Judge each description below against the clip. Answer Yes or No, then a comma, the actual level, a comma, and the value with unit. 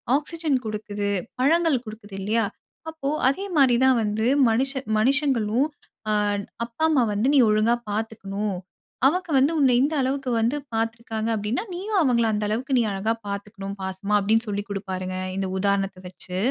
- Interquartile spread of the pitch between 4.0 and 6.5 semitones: Yes, average, 4.7 semitones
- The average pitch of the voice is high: Yes, high, 225 Hz